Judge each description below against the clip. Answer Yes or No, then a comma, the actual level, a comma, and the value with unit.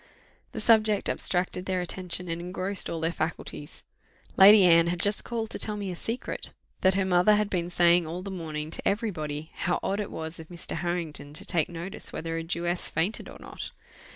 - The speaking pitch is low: No, medium, 175 Hz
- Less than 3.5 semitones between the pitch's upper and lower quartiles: Yes, average, 2.9 semitones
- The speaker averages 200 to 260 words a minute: Yes, fast, 205 wpm